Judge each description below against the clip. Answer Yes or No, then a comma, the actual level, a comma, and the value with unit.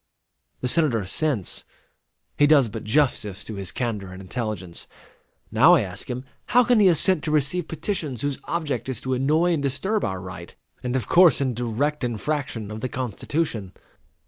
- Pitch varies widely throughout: Yes, wide, 6.2 semitones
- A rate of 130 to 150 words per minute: No, average, 170 wpm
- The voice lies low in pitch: Yes, low, 130 Hz